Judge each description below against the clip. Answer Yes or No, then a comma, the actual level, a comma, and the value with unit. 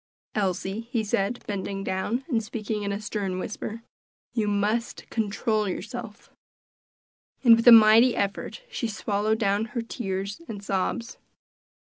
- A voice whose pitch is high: Yes, high, 215 Hz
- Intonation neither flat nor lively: No, narrow, 2.3 semitones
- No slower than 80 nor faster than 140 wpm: Yes, slow, 135 wpm